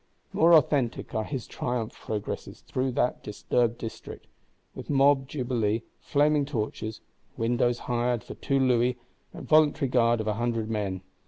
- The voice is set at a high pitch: No, low, 120 Hz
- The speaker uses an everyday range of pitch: Yes, average, 3.2 semitones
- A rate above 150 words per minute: No, average, 145 wpm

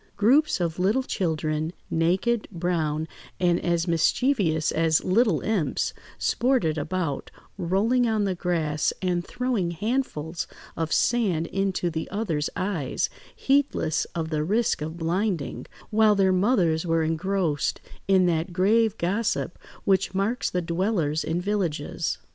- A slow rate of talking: Yes, slow, 130 wpm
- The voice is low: No, medium, 180 Hz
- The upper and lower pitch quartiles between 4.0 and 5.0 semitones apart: Yes, average, 4.3 semitones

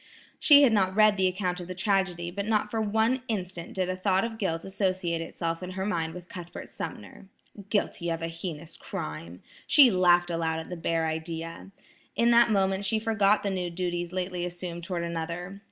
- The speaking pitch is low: No, medium, 180 Hz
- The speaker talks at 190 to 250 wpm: Yes, average, 195 wpm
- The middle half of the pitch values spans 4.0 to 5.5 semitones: No, average, 3.0 semitones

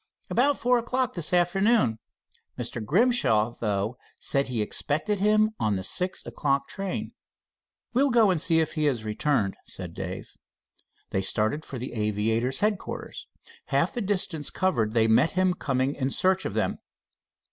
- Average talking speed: Yes, average, 155 wpm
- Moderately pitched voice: Yes, medium, 150 Hz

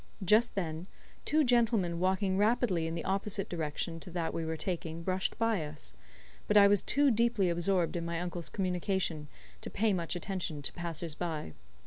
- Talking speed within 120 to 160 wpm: No, average, 175 wpm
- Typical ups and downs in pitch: Yes, average, 3.4 semitones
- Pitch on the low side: No, medium, 180 Hz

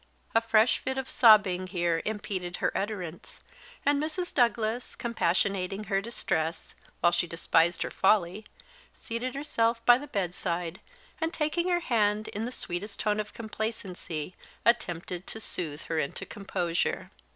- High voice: Yes, high, 210 Hz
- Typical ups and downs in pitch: Yes, average, 4.8 semitones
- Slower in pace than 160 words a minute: Yes, average, 140 wpm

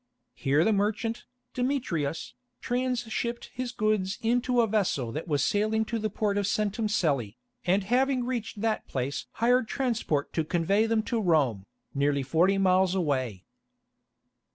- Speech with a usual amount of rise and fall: No, wide, 6.5 semitones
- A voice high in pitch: Yes, high, 205 Hz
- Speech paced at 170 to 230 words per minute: No, average, 145 wpm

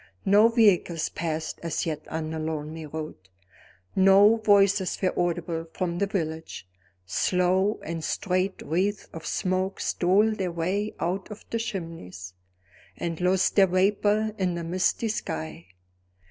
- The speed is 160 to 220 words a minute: No, slow, 135 wpm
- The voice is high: No, medium, 180 Hz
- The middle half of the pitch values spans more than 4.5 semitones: No, average, 3.5 semitones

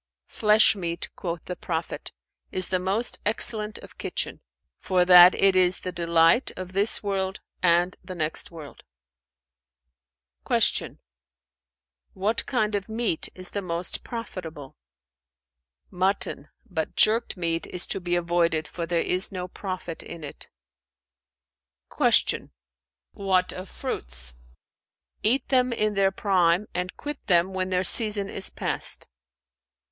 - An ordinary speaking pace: No, slow, 130 wpm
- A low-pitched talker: No, medium, 185 Hz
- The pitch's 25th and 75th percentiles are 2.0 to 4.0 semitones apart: Yes, average, 2.9 semitones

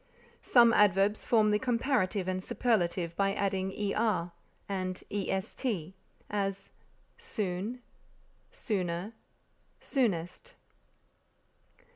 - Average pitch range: Yes, average, 3.2 semitones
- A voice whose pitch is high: Yes, high, 195 Hz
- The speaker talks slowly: Yes, slow, 80 wpm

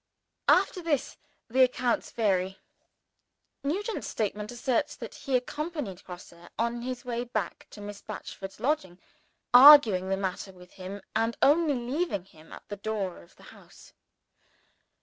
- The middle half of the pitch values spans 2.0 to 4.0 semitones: No, wide, 5.5 semitones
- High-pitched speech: Yes, high, 230 Hz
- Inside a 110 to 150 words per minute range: Yes, average, 140 wpm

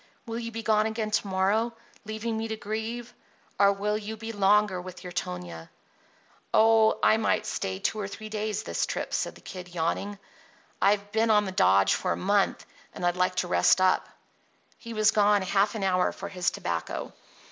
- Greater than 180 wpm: Yes, average, 190 wpm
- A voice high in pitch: Yes, high, 205 Hz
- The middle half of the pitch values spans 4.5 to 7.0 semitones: No, average, 2.9 semitones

